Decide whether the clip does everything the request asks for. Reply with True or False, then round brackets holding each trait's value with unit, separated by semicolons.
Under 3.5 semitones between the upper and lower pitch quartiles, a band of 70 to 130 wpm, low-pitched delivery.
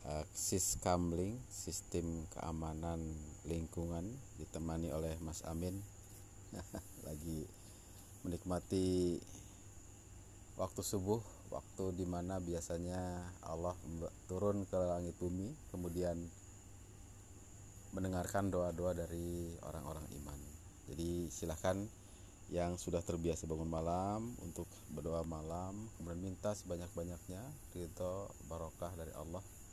True (2.8 semitones; 90 wpm; 90 Hz)